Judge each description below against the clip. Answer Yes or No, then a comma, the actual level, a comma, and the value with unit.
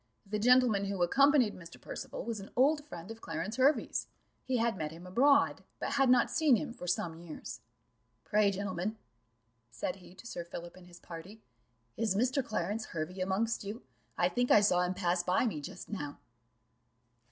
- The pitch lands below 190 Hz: No, high, 205 Hz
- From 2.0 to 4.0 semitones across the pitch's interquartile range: No, average, 5.3 semitones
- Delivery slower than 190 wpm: Yes, average, 180 wpm